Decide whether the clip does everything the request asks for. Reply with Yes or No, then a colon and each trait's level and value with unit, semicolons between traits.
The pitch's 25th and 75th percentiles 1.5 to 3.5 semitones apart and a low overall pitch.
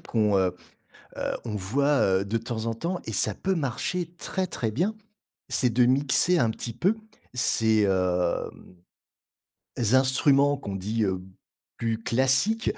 No: average, 5.1 semitones; low, 120 Hz